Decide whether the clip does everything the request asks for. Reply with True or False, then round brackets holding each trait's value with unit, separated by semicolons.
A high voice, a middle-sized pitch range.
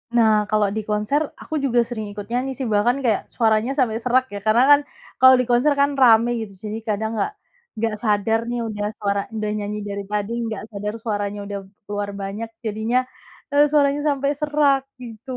True (220 Hz; 3.6 semitones)